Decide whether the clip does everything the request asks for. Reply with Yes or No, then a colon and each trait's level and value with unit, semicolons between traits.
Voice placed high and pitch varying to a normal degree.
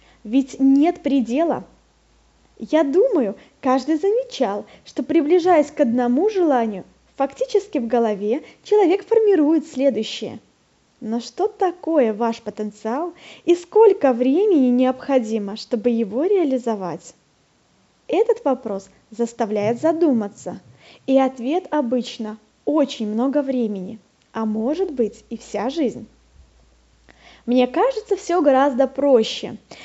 No: very high, 265 Hz; wide, 6.3 semitones